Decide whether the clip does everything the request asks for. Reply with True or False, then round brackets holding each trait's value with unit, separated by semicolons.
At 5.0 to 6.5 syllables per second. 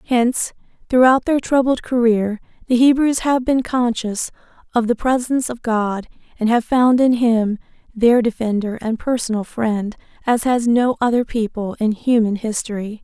False (4.6 syllables/s)